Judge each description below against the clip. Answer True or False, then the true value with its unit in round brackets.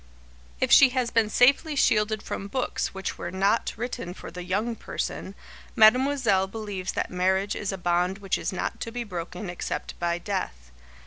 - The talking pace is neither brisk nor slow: True (175 wpm)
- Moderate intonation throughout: True (4.0 semitones)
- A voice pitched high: True (200 Hz)